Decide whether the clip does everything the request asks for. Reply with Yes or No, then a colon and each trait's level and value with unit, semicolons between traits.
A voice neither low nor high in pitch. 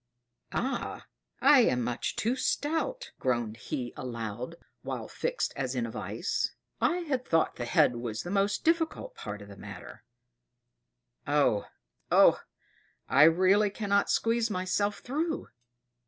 Yes: medium, 180 Hz